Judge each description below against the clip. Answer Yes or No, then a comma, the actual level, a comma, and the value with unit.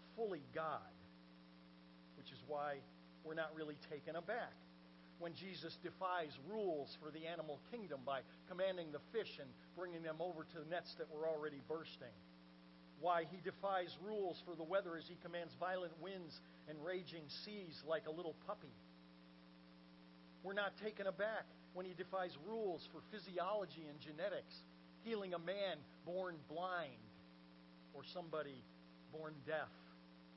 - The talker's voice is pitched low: No, medium, 160 Hz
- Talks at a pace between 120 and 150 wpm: Yes, average, 145 wpm